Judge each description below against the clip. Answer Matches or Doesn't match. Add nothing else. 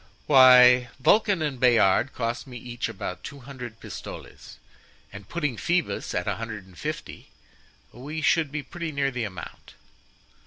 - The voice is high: Doesn't match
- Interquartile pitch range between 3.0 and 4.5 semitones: Matches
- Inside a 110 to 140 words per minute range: Doesn't match